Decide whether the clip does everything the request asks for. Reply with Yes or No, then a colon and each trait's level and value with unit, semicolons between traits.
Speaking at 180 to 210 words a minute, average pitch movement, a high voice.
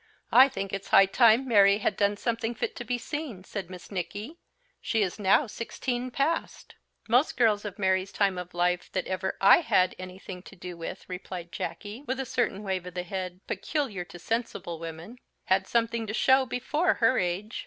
Yes: average, 190 wpm; average, 4.6 semitones; high, 205 Hz